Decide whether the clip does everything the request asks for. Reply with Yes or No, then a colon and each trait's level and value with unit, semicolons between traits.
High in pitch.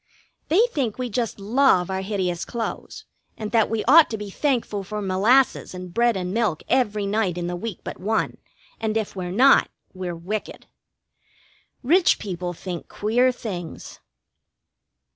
Yes: high, 210 Hz